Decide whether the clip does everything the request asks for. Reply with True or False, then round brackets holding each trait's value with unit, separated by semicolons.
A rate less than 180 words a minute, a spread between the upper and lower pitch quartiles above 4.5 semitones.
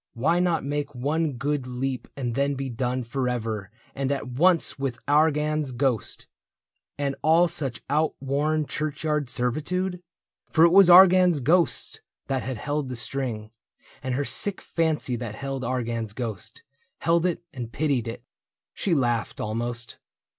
False (145 wpm; 4.1 semitones)